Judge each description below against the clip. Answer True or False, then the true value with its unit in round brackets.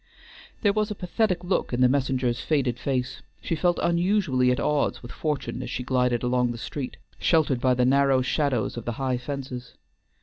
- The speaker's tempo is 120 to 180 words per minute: False (190 wpm)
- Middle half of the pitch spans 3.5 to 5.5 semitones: True (4.0 semitones)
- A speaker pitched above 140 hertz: False (130 Hz)